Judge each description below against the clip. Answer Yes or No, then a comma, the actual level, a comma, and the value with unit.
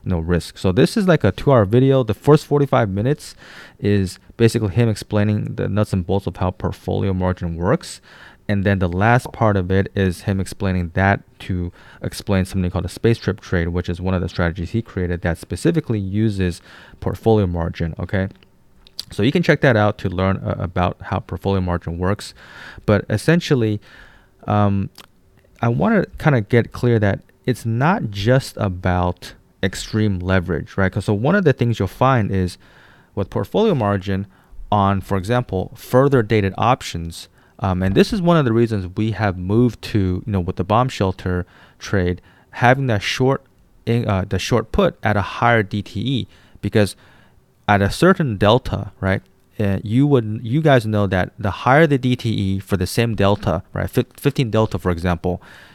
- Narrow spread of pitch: No, average, 4.3 semitones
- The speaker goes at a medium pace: Yes, average, 180 wpm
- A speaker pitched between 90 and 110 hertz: Yes, low, 100 Hz